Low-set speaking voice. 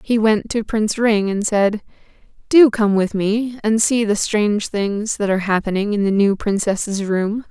No: high, 210 Hz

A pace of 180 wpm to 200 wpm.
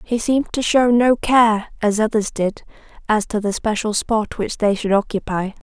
Yes: average, 190 wpm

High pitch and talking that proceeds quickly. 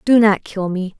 Yes: high, 200 Hz; fast, 240 wpm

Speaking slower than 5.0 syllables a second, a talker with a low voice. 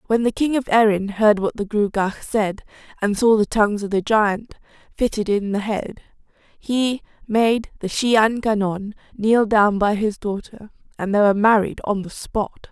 No: 4.5 syllables/s; high, 210 Hz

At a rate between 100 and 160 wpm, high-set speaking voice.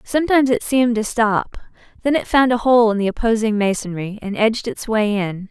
No: fast, 205 wpm; high, 225 Hz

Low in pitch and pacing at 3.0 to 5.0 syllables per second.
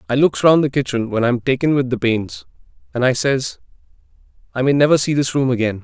No: low, 130 Hz; 5.9 syllables/s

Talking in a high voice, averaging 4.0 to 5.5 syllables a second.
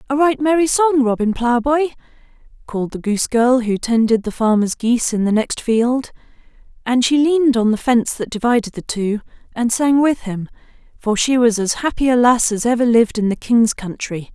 Yes: high, 240 Hz; 5.3 syllables/s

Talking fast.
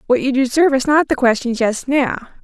Yes: fast, 220 wpm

